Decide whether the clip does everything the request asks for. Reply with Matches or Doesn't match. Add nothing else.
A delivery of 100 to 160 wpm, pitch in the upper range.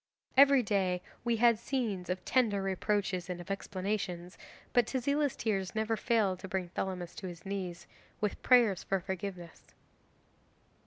Matches